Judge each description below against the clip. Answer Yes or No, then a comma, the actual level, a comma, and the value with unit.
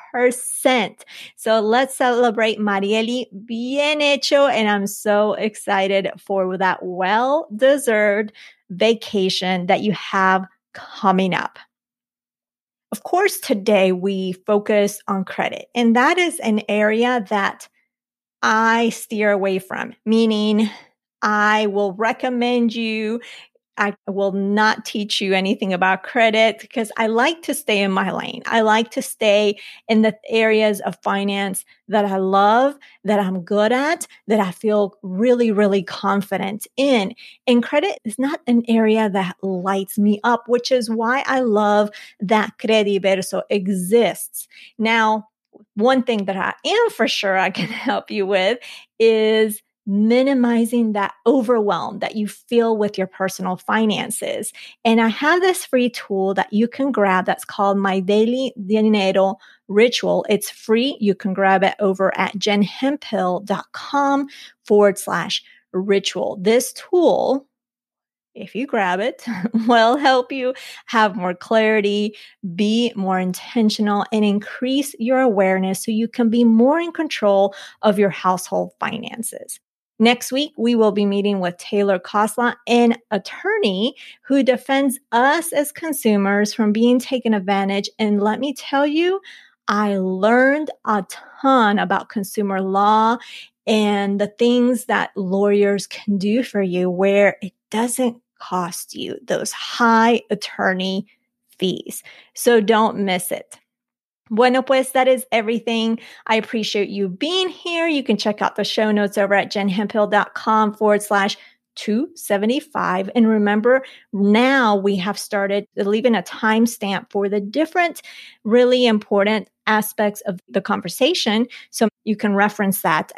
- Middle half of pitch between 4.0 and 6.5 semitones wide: No, average, 3.2 semitones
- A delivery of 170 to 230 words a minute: No, slow, 135 wpm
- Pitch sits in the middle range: No, high, 215 Hz